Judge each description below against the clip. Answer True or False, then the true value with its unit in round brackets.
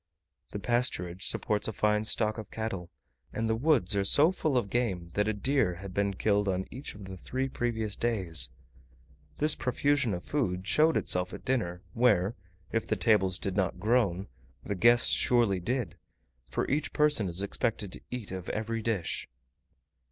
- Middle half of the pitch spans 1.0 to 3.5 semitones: False (4.3 semitones)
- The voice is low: True (105 Hz)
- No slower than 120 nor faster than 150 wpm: False (175 wpm)